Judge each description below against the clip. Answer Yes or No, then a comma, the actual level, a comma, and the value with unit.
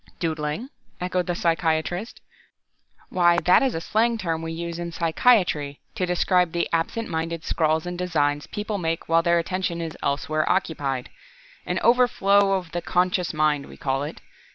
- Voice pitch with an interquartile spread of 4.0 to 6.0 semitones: No, narrow, 2.4 semitones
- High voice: No, medium, 170 Hz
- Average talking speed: Yes, average, 160 wpm